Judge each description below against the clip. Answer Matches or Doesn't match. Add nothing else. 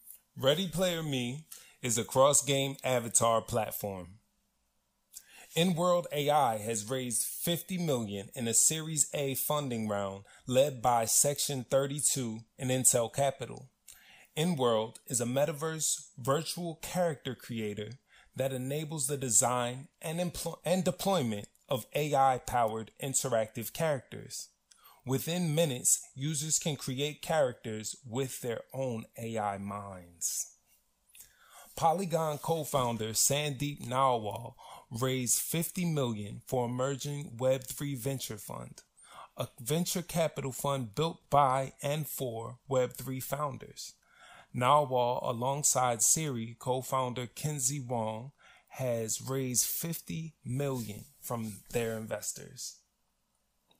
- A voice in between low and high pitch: Doesn't match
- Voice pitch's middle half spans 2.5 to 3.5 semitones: Doesn't match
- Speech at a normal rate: Doesn't match